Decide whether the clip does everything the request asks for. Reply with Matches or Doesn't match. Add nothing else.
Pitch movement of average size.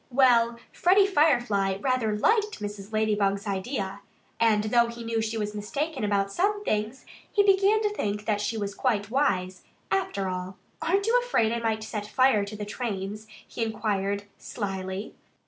Matches